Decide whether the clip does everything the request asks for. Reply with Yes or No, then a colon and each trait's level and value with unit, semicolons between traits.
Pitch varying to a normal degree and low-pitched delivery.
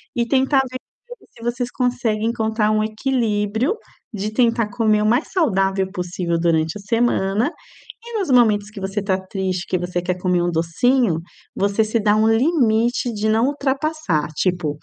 No: average, 4.2 semitones; high, 215 Hz